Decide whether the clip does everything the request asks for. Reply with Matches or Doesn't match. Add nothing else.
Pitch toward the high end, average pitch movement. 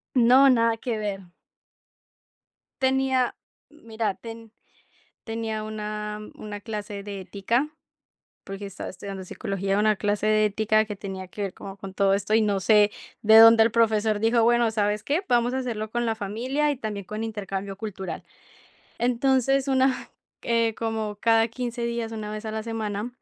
Doesn't match